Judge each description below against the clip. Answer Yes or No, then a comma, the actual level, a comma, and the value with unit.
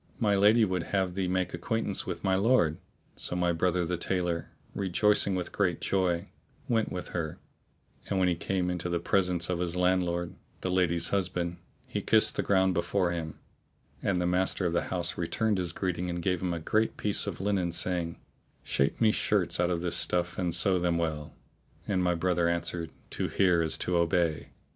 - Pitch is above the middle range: No, very low, 90 Hz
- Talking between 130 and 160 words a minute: No, average, 190 wpm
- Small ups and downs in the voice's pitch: Yes, narrow, 1.7 semitones